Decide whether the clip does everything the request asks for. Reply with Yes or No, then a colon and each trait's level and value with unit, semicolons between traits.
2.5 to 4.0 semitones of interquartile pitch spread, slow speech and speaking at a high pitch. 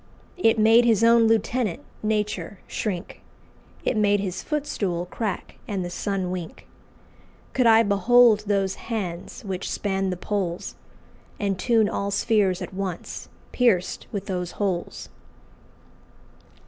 Yes: average, 3.2 semitones; slow, 125 wpm; high, 200 Hz